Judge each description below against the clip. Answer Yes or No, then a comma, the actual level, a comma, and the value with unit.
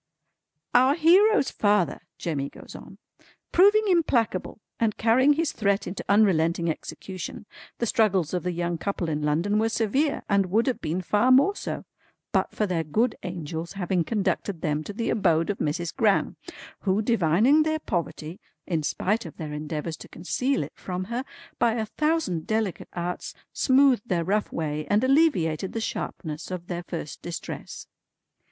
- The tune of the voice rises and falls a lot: Yes, wide, 5.7 semitones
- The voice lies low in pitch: No, high, 195 Hz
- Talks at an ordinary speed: Yes, average, 160 wpm